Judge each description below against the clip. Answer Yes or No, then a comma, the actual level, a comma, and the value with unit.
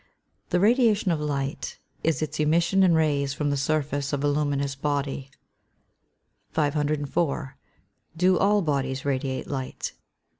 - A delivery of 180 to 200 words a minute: No, slow, 135 wpm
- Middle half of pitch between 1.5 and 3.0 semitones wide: Yes, average, 2.7 semitones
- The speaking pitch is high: No, medium, 145 Hz